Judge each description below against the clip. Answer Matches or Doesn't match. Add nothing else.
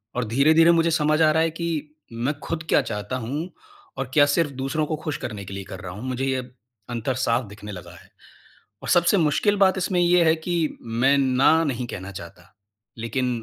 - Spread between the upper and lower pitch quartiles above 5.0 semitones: Matches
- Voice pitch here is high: Doesn't match